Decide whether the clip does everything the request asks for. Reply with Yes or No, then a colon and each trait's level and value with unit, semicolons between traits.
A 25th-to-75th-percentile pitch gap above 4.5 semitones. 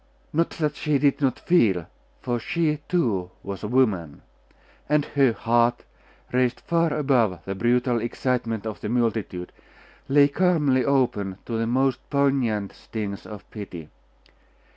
Yes: average, 4.9 semitones